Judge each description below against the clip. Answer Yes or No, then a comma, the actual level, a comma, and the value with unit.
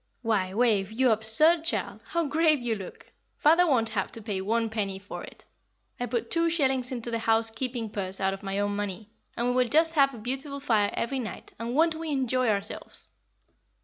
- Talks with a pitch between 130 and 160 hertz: No, high, 235 Hz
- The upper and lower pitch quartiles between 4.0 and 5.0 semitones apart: Yes, average, 4.5 semitones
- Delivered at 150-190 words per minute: No, average, 200 wpm